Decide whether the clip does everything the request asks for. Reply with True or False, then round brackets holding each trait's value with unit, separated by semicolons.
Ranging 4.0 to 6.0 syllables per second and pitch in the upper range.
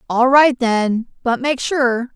False (3.4 syllables/s; 250 Hz)